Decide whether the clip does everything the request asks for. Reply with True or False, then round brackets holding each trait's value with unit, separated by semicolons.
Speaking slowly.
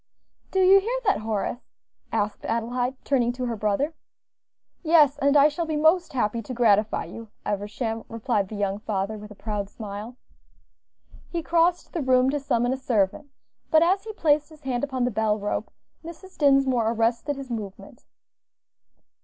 False (165 wpm)